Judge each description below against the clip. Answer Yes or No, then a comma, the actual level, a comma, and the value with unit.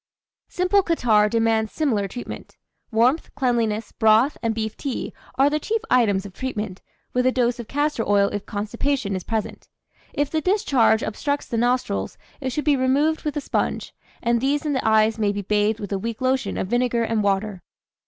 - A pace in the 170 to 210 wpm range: Yes, average, 185 wpm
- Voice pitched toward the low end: No, high, 235 Hz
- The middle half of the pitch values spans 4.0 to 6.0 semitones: Yes, average, 4.5 semitones